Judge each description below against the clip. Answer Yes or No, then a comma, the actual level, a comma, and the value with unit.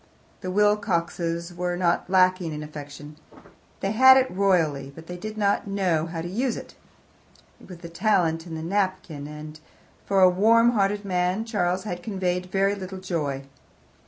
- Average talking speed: Yes, average, 165 wpm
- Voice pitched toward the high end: No, medium, 180 Hz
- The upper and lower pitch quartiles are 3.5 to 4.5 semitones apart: No, average, 3.1 semitones